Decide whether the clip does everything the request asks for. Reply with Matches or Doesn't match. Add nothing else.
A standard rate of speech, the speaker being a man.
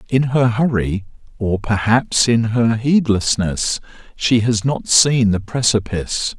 Doesn't match